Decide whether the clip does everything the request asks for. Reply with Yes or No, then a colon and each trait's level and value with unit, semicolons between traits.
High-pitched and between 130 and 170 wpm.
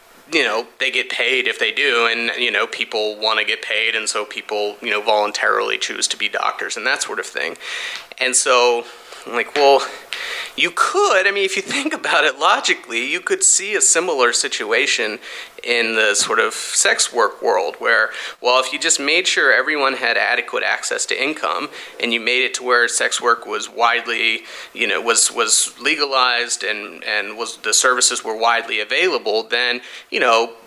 No: very high, 370 Hz; average, 190 wpm